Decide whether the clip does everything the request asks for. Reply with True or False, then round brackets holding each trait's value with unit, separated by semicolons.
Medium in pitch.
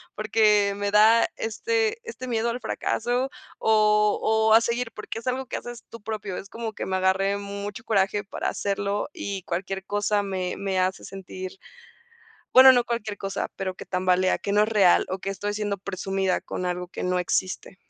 False (205 Hz)